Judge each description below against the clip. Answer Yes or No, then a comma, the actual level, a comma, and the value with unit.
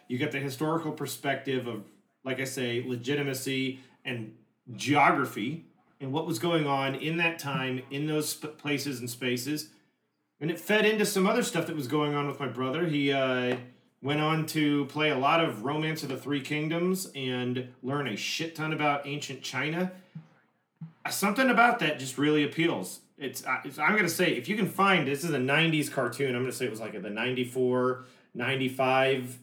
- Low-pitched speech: No, medium, 145 Hz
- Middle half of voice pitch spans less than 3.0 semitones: No, average, 3.5 semitones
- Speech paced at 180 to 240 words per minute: Yes, average, 190 wpm